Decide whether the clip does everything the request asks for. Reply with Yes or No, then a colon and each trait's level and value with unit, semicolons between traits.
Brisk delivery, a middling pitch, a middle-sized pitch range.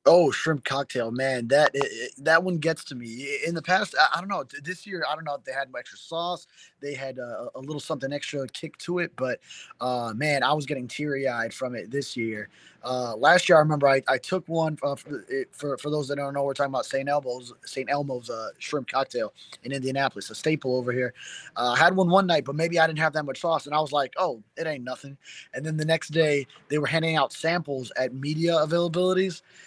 Yes: fast, 240 wpm; medium, 145 Hz; average, 3.5 semitones